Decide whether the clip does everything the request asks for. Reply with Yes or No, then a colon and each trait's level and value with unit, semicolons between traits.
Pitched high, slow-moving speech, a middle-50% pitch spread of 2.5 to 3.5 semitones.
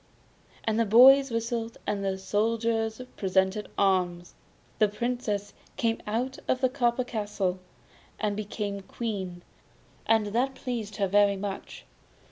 Yes: high, 215 Hz; slow, 125 wpm; average, 2.8 semitones